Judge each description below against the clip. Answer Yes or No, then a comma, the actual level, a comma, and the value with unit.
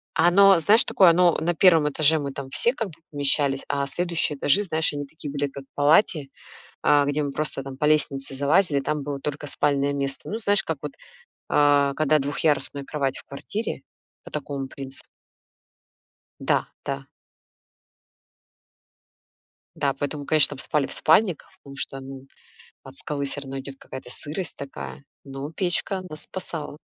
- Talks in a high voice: No, medium, 145 Hz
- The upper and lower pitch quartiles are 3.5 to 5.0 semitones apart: No, narrow, 2.5 semitones